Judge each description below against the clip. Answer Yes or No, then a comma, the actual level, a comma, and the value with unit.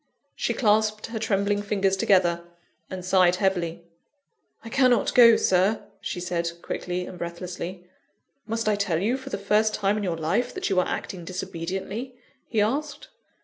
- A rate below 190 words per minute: Yes, average, 160 wpm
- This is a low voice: No, high, 195 Hz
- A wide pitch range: No, average, 3.3 semitones